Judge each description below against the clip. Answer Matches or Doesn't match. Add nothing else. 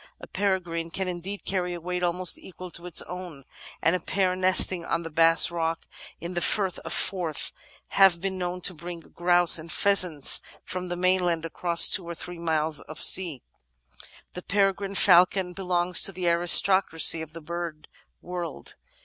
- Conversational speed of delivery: Matches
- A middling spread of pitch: Doesn't match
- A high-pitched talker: Doesn't match